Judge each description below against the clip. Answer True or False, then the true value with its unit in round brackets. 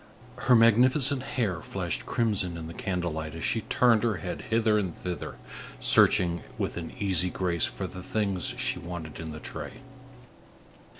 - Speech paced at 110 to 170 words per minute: True (165 wpm)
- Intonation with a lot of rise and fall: False (5.0 semitones)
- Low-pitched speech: True (95 Hz)